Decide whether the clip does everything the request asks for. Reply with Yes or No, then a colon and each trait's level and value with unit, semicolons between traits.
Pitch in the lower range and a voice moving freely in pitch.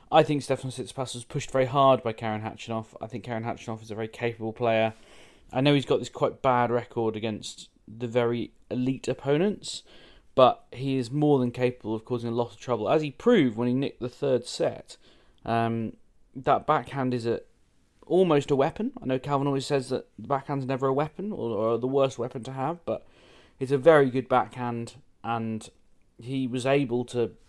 No: low, 125 Hz; average, 2.9 semitones